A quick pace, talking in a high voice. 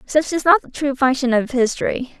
Yes: fast, 220 wpm; very high, 270 Hz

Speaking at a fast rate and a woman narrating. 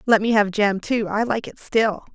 Yes: fast, 250 wpm; female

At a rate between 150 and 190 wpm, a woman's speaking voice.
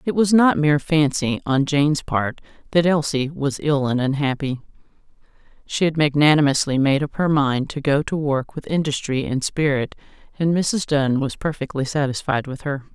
Yes: average, 170 wpm; female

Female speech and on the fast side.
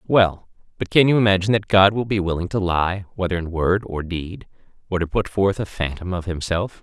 No: male; fast, 220 wpm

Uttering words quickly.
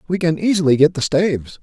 Yes: fast, 220 wpm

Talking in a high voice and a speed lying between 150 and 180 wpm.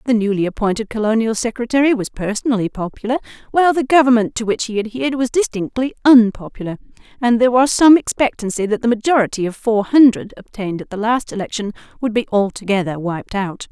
Yes: high, 225 Hz; average, 170 wpm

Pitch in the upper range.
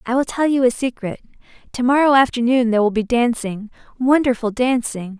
Yes: high, 245 Hz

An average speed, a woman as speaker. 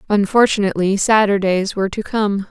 Yes: average, 145 wpm; female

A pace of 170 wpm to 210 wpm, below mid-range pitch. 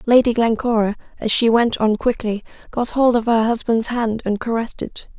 No: average, 185 wpm; high, 230 Hz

